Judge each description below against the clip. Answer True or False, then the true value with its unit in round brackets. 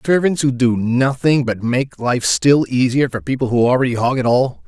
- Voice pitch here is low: True (125 Hz)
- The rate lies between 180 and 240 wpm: True (205 wpm)